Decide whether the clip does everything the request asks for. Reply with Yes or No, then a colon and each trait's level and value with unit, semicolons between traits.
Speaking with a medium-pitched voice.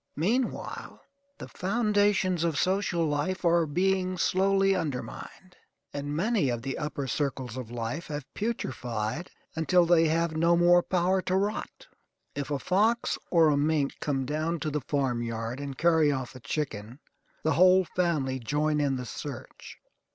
Yes: medium, 160 Hz